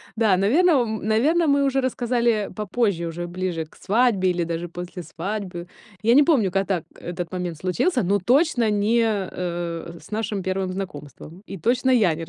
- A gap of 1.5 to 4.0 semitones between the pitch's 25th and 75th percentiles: No, average, 5.1 semitones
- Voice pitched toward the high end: Yes, high, 195 Hz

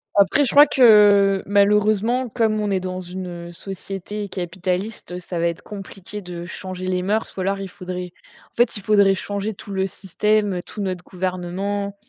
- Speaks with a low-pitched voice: No, high, 195 Hz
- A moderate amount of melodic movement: No, narrow, 2.2 semitones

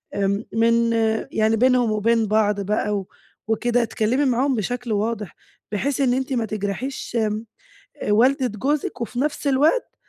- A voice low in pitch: No, high, 230 Hz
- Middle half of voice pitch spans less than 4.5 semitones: Yes, average, 3.3 semitones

